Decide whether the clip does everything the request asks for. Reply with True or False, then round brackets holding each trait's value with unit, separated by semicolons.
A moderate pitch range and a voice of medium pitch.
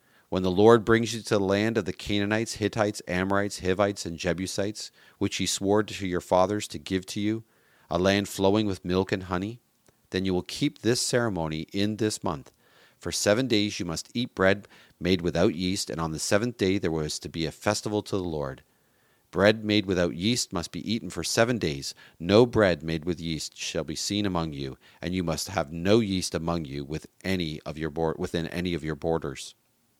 False (3.7 semitones; 95 Hz)